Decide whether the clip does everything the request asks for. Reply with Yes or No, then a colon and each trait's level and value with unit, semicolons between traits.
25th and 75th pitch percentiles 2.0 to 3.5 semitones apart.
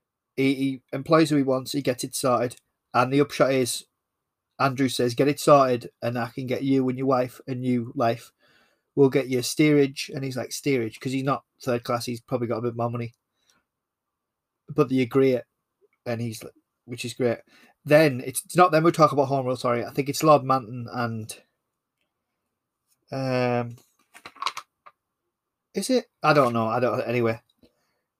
Yes: average, 2.8 semitones